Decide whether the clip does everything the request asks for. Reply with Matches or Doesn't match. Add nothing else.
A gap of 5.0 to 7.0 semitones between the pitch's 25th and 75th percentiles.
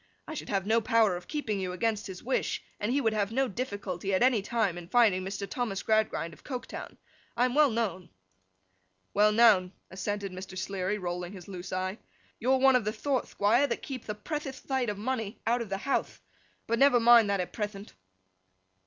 Doesn't match